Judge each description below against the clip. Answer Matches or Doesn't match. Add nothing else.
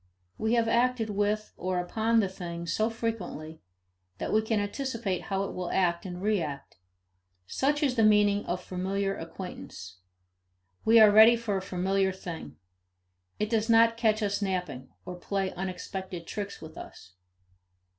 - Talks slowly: Doesn't match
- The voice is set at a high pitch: Matches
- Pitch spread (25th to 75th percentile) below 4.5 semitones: Matches